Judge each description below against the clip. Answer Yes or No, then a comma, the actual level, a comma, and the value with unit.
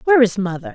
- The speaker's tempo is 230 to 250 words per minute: Yes, fast, 240 wpm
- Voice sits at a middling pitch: No, high, 225 Hz